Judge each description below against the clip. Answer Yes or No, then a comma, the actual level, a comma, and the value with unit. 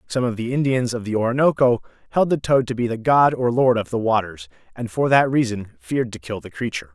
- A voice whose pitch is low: Yes, low, 120 Hz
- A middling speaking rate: No, fast, 240 wpm